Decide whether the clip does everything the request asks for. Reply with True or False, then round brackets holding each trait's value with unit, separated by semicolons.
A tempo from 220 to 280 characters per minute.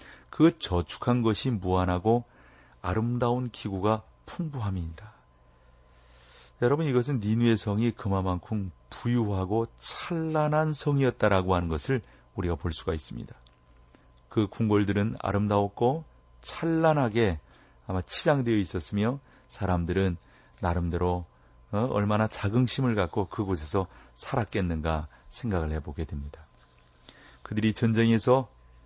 True (270 characters per minute)